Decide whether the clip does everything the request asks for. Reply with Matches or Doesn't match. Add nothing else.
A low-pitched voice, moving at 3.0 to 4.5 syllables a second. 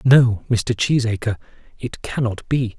Matches